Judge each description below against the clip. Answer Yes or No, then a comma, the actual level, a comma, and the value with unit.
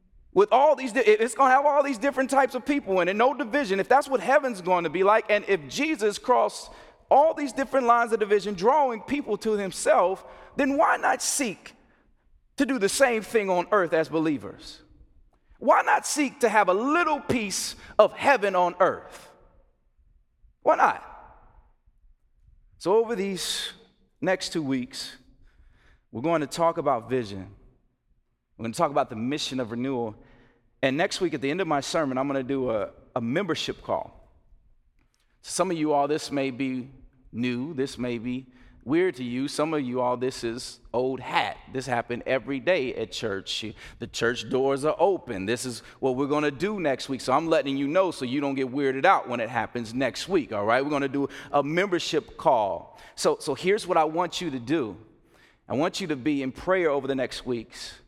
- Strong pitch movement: Yes, wide, 8.4 semitones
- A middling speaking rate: Yes, average, 190 wpm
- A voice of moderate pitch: Yes, medium, 155 Hz